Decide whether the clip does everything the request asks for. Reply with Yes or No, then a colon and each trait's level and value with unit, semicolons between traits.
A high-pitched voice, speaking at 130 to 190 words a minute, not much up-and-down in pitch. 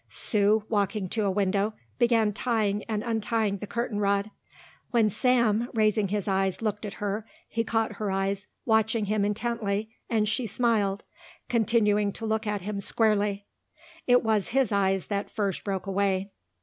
Yes: high, 210 Hz; average, 160 wpm; narrow, 1.9 semitones